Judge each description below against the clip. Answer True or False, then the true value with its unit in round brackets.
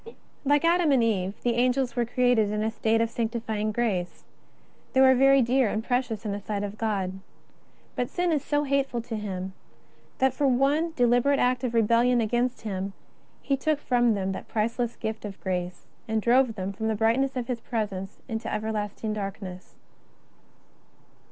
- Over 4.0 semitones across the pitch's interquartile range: False (3.3 semitones)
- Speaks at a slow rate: False (175 wpm)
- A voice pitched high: True (230 Hz)